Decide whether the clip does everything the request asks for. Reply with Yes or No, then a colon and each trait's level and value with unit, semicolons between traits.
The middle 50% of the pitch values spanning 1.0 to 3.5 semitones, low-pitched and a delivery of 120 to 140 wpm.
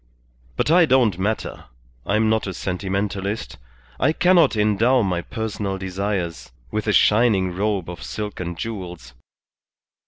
Yes: average, 3.0 semitones; low, 100 Hz; slow, 135 wpm